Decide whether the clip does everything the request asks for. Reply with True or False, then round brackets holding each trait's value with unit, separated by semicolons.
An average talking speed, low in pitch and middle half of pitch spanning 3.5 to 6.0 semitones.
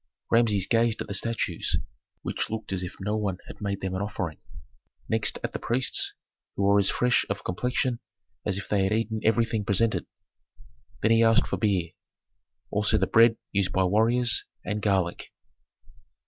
False (170 wpm; 105 Hz; 2.7 semitones)